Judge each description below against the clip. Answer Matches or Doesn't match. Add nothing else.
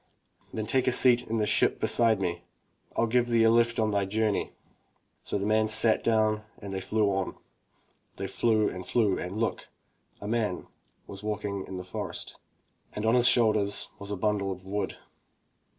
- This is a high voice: Doesn't match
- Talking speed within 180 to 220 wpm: Matches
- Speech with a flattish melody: Matches